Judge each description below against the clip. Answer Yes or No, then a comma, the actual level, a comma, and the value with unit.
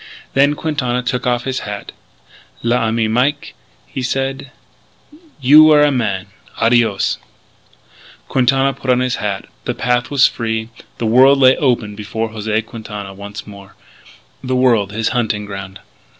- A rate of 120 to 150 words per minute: Yes, average, 140 wpm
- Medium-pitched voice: No, low, 120 Hz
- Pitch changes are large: No, average, 3.8 semitones